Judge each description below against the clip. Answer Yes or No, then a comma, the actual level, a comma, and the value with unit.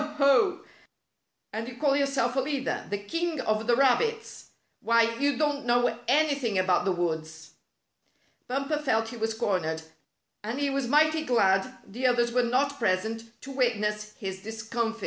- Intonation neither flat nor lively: Yes, average, 4.3 semitones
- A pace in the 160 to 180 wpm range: Yes, average, 165 wpm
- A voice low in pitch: No, high, 240 Hz